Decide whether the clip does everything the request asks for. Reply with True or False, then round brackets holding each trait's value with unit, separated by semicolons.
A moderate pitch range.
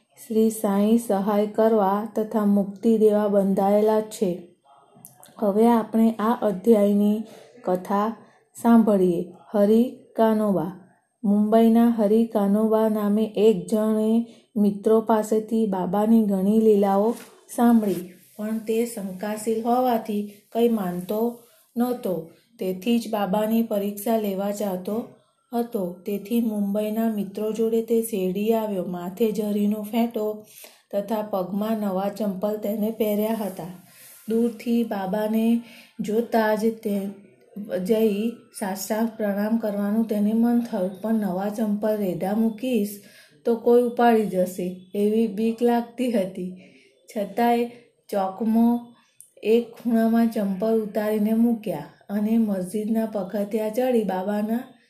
False (2.0 semitones)